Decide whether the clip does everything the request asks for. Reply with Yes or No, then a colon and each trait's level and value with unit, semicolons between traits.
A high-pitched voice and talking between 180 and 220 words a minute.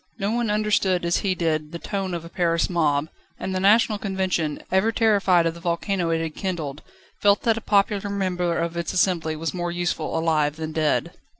No: medium, 175 Hz; average, 200 wpm